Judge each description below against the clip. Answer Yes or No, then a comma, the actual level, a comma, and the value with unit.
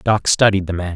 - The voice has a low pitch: Yes, very low, 95 Hz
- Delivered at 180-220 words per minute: No, fast, 250 wpm